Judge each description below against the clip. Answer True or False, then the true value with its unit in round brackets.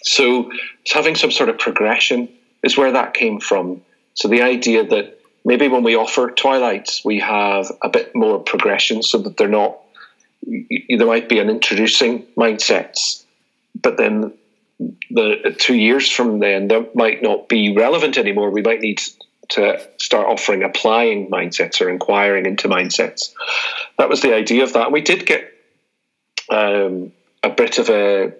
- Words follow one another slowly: False (165 wpm)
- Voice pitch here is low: True (120 Hz)